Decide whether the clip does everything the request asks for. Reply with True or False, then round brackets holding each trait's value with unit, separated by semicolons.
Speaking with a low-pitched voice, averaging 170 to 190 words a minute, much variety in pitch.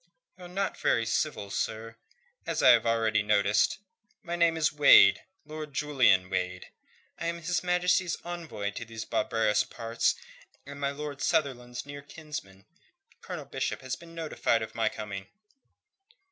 False (130 Hz; 145 wpm; 6.5 semitones)